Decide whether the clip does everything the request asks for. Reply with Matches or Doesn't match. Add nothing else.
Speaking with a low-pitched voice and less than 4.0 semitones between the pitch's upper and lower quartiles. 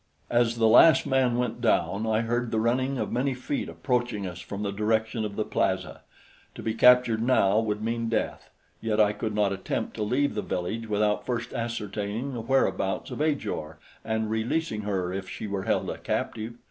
Matches